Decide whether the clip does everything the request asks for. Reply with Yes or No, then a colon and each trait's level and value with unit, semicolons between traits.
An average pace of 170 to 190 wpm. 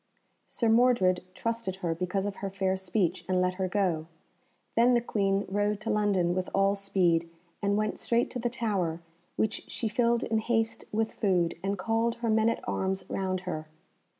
Yes: average, 180 wpm